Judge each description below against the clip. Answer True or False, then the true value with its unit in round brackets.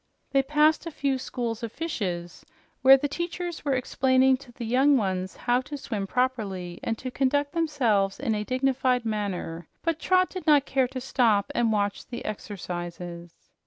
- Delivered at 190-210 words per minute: False (170 wpm)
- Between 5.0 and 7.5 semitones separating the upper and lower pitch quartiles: True (5.3 semitones)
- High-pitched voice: True (250 Hz)